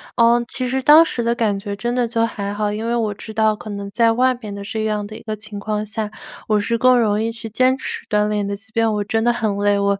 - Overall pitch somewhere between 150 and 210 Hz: No, high, 220 Hz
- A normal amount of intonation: No, narrow, 2.3 semitones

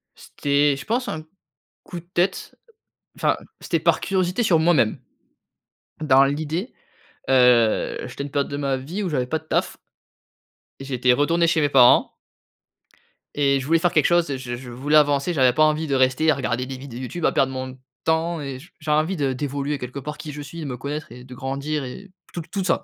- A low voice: No, medium, 145 Hz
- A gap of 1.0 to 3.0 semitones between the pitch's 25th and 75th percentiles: No, average, 3.5 semitones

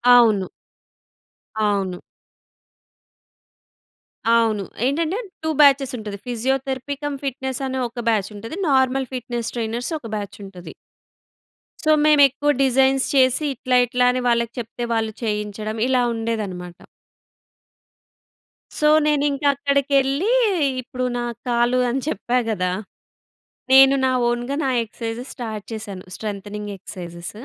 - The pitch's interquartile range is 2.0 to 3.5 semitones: No, average, 3.9 semitones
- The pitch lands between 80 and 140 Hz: No, high, 240 Hz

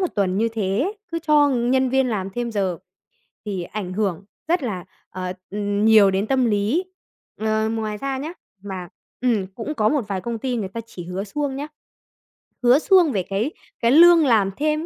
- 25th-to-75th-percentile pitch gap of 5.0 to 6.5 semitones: Yes, average, 5.3 semitones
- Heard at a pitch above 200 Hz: Yes, high, 220 Hz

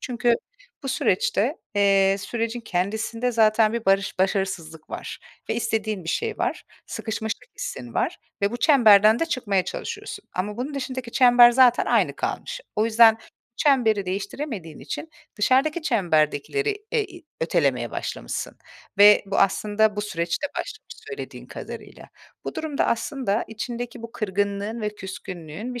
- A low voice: No, high, 220 Hz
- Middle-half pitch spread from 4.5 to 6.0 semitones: No, average, 4.0 semitones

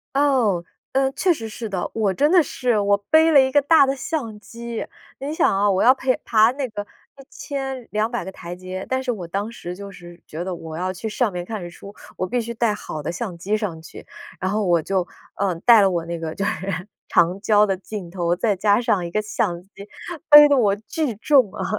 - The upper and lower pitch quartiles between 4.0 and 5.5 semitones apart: Yes, average, 5.2 semitones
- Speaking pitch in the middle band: No, high, 210 Hz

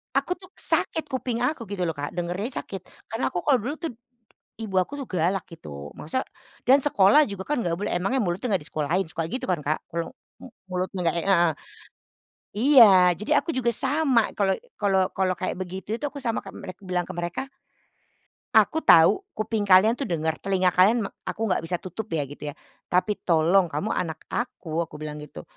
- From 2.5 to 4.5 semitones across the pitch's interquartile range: No, average, 5.1 semitones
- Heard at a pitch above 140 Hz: Yes, high, 190 Hz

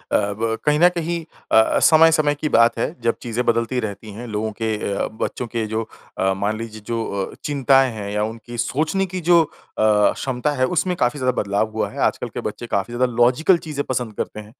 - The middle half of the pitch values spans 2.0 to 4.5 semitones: No, average, 5.0 semitones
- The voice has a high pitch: No, low, 120 Hz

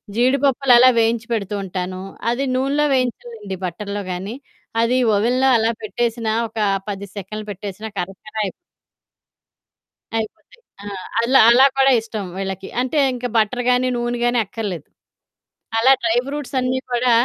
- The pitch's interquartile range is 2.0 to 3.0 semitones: No, average, 3.8 semitones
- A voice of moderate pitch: No, high, 230 Hz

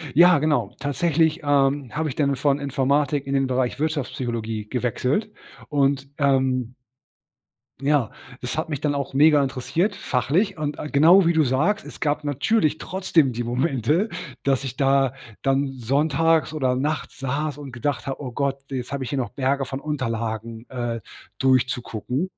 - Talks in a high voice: No, medium, 140 Hz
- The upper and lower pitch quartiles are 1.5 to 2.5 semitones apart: No, average, 2.9 semitones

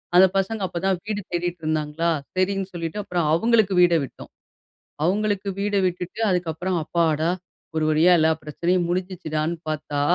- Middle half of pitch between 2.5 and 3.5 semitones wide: Yes, average, 3.0 semitones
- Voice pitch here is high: No, medium, 175 Hz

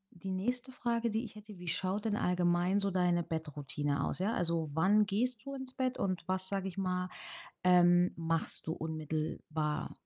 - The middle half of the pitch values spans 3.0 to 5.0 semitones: Yes, average, 4.2 semitones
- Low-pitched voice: No, medium, 180 Hz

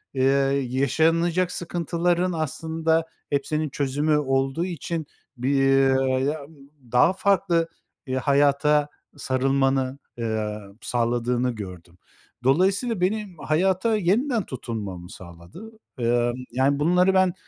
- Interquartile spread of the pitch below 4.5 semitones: No, average, 5.2 semitones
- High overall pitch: No, medium, 145 Hz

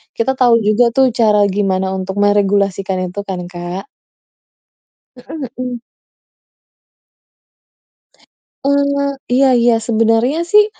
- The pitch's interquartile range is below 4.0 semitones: No, average, 4.8 semitones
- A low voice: No, high, 225 Hz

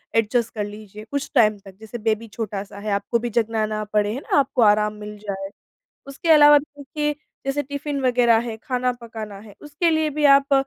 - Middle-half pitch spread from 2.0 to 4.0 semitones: No, average, 4.7 semitones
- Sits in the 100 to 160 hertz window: No, high, 230 Hz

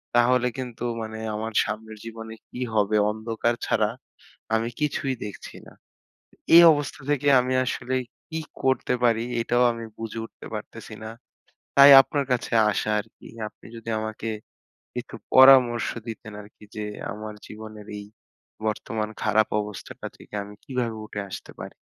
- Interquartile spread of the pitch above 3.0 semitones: No, narrow, 2.6 semitones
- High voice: No, low, 115 Hz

